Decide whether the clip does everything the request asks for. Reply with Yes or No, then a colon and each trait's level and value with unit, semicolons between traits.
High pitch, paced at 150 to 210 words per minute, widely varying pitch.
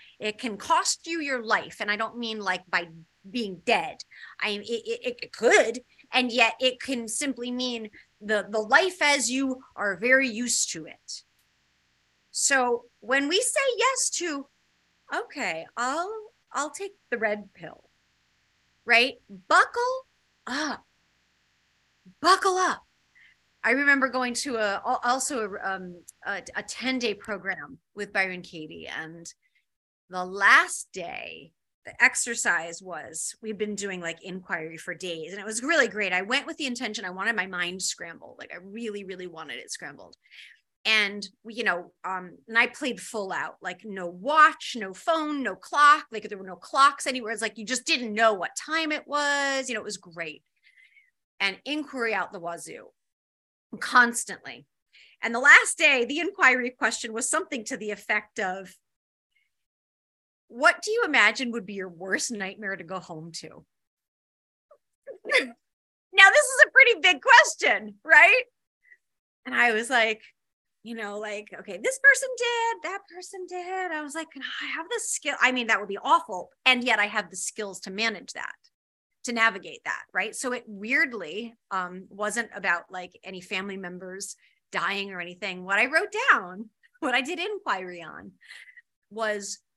Yes: high, 230 Hz; average, 165 wpm; wide, 6.6 semitones